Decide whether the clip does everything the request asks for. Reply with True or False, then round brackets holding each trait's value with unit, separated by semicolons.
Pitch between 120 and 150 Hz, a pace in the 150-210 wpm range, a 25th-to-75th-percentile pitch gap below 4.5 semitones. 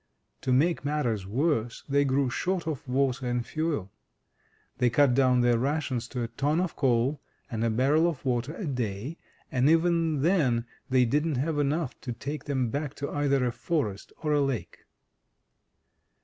True (135 Hz; 170 wpm; 3.7 semitones)